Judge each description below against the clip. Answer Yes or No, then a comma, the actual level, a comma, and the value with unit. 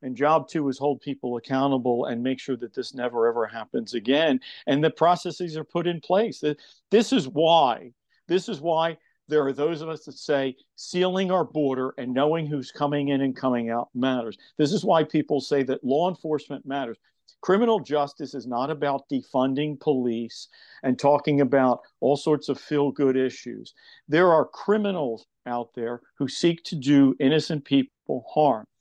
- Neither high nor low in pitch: Yes, medium, 145 Hz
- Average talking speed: Yes, average, 175 wpm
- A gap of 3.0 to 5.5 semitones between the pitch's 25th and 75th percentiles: Yes, average, 3.6 semitones